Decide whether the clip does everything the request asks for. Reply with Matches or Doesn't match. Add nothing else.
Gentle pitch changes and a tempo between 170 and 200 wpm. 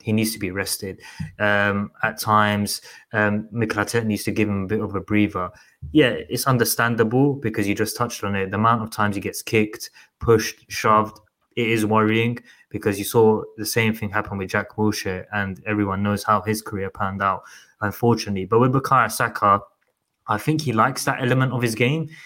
Matches